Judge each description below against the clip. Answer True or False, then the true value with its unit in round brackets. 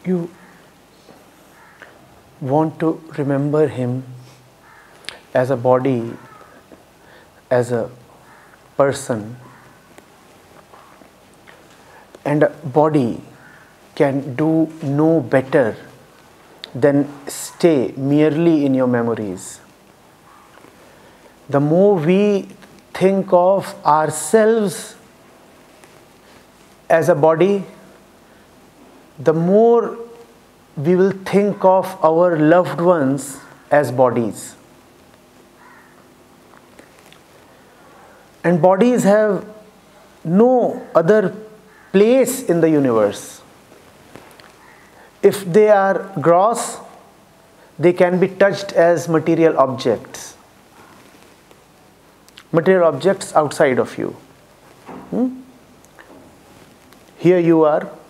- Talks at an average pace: False (75 wpm)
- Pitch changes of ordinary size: False (5.8 semitones)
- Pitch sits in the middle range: True (165 Hz)